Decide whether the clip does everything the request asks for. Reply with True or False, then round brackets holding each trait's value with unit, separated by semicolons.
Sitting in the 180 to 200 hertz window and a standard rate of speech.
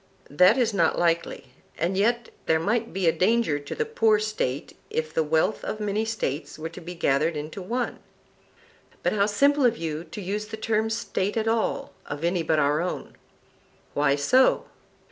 True (190 Hz; 185 wpm)